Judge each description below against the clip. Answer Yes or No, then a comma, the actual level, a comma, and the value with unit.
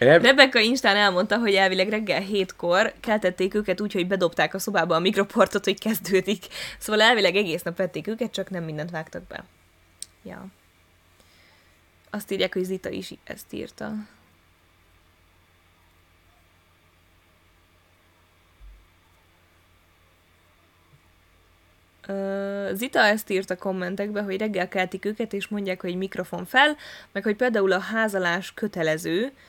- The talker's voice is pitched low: No, medium, 180 Hz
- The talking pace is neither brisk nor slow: Yes, average, 120 wpm